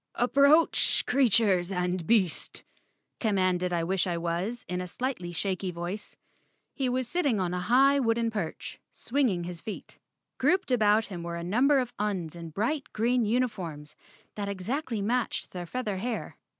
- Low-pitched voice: No, high, 205 Hz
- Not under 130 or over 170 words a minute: Yes, average, 160 wpm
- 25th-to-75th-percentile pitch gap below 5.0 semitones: No, wide, 5.6 semitones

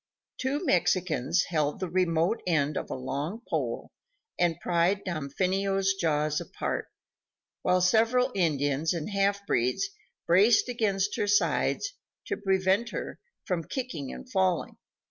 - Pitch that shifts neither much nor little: Yes, average, 4.0 semitones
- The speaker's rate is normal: No, slow, 125 wpm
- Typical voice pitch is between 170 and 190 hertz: Yes, medium, 185 Hz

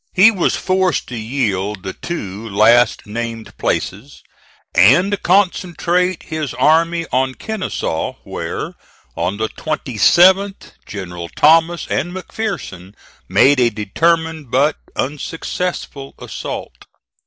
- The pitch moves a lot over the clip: Yes, wide, 8.2 semitones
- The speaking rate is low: Yes, slow, 105 wpm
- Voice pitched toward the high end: No, medium, 140 Hz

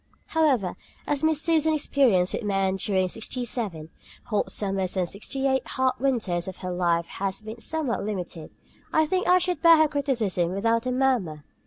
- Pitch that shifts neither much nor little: No, wide, 7.0 semitones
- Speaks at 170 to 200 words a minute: Yes, average, 180 wpm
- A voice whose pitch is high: Yes, high, 225 Hz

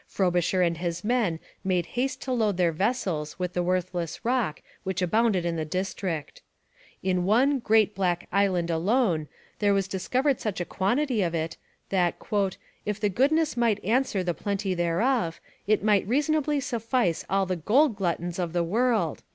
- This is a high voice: Yes, high, 195 Hz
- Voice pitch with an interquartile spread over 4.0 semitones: Yes, average, 5.1 semitones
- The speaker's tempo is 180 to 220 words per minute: No, average, 165 wpm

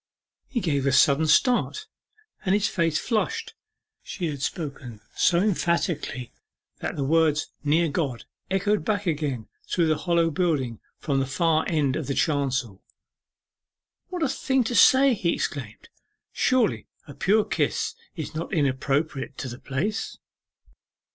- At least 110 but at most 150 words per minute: Yes, average, 140 wpm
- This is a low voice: No, medium, 160 Hz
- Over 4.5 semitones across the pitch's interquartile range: Yes, wide, 5.6 semitones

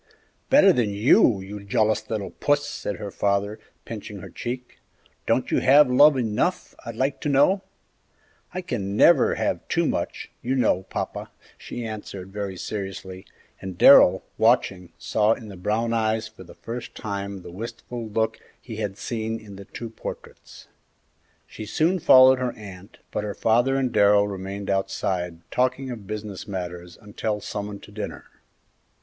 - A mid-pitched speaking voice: No, low, 110 Hz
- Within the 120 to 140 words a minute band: No, average, 160 wpm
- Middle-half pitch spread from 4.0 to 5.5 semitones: No, average, 3.6 semitones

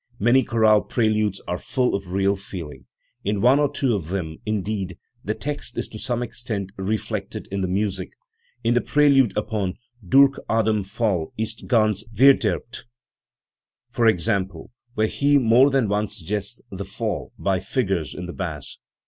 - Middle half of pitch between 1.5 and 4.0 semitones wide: Yes, average, 3.7 semitones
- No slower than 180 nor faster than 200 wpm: No, average, 165 wpm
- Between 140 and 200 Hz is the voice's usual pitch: No, low, 105 Hz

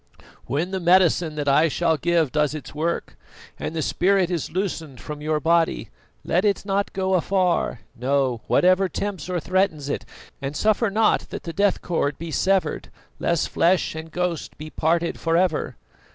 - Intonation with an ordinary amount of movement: Yes, average, 3.6 semitones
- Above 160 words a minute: Yes, average, 170 wpm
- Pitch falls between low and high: Yes, medium, 170 Hz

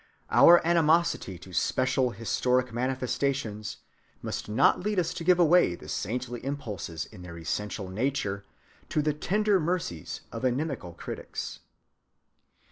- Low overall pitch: Yes, low, 130 Hz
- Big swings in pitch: Yes, wide, 7.5 semitones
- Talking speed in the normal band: No, slow, 125 wpm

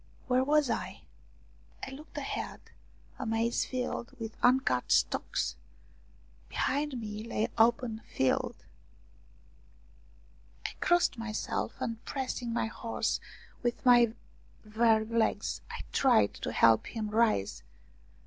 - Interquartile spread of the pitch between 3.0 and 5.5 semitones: No, narrow, 2.6 semitones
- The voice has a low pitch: No, high, 230 Hz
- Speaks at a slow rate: Yes, slow, 110 wpm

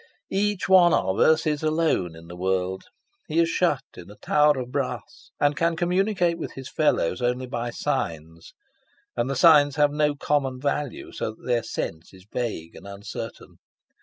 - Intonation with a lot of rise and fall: Yes, wide, 8.0 semitones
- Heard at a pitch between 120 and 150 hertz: Yes, low, 135 Hz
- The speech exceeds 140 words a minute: Yes, average, 175 wpm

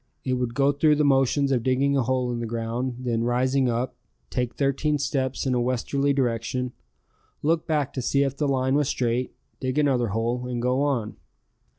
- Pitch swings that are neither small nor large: No, narrow, 2.3 semitones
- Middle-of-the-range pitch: No, low, 130 Hz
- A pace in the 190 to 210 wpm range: Yes, average, 195 wpm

